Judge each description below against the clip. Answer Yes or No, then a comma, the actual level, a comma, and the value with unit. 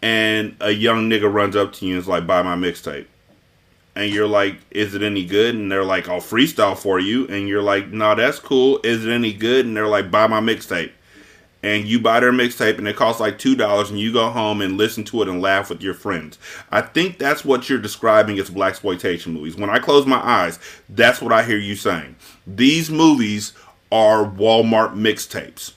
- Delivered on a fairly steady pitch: Yes, narrow, 2.2 semitones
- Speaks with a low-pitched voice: Yes, low, 105 Hz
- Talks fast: Yes, fast, 215 wpm